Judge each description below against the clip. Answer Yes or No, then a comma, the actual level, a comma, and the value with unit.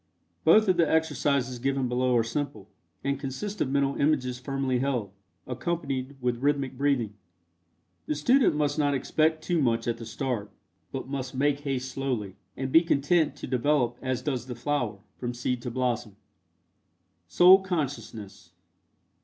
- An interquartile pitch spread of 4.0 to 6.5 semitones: No, average, 2.9 semitones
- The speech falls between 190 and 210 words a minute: No, average, 155 wpm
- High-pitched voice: No, low, 135 Hz